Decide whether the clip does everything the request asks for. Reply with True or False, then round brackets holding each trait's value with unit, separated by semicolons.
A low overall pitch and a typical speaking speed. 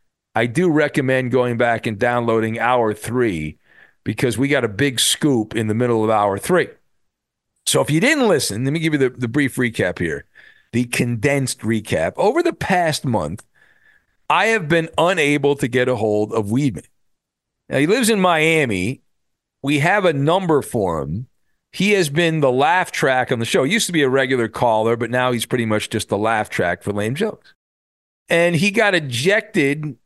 True (125 Hz; 190 wpm)